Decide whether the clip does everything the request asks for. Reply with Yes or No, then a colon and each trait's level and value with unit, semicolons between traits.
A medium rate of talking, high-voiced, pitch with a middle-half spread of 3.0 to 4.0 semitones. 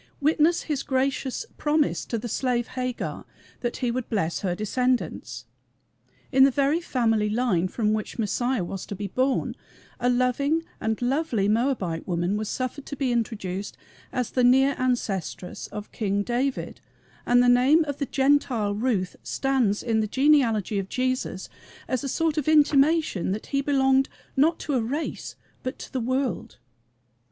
No: average, 160 wpm; very high, 250 Hz; average, 4.4 semitones